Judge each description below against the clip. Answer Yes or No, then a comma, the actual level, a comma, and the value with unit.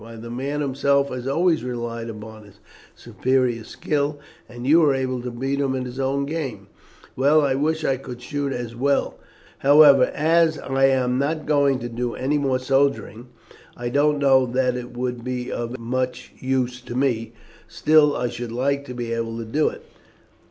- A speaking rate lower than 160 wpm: No, average, 185 wpm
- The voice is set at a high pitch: No, low, 130 Hz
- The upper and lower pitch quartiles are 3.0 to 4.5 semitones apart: No, narrow, 2.6 semitones